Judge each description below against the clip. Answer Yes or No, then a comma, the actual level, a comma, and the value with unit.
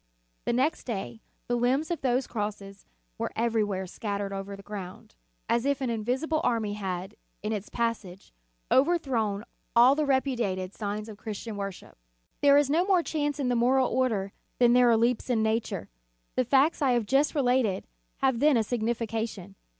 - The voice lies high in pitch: Yes, high, 235 Hz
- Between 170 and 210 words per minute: Yes, average, 175 wpm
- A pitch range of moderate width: Yes, average, 4.3 semitones